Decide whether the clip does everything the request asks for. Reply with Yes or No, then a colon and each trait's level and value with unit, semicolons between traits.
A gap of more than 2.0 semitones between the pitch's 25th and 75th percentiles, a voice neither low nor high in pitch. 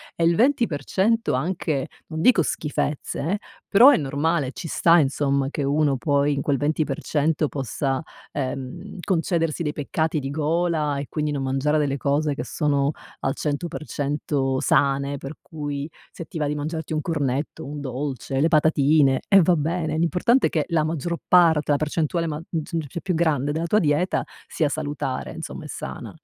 Yes: average, 2.7 semitones; medium, 150 Hz